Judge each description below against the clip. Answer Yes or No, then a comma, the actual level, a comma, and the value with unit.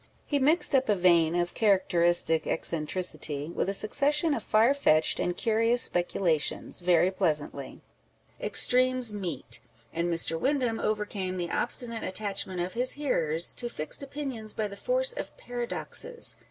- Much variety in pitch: Yes, wide, 6.4 semitones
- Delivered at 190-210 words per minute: No, average, 145 wpm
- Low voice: No, high, 200 Hz